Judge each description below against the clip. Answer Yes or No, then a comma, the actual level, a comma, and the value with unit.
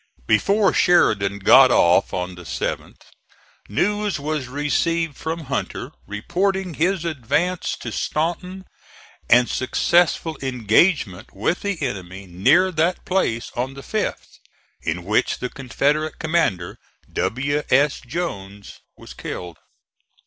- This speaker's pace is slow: Yes, slow, 115 wpm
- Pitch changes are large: Yes, wide, 8.7 semitones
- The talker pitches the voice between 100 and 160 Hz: Yes, medium, 140 Hz